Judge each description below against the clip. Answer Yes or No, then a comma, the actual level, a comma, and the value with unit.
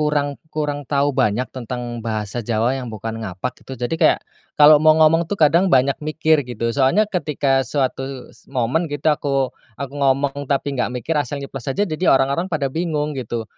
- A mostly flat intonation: No, average, 3.3 semitones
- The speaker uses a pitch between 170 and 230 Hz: No, medium, 140 Hz